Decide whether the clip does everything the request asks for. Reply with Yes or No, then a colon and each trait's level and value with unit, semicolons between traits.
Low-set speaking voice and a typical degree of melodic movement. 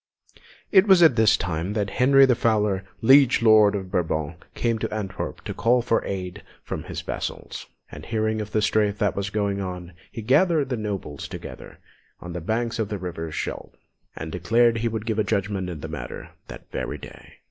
Yes: low, 105 Hz; average, 3.7 semitones